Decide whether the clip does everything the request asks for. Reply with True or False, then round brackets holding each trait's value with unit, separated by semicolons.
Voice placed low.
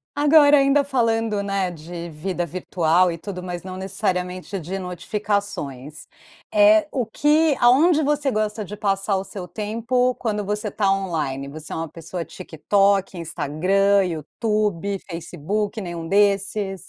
False (195 Hz)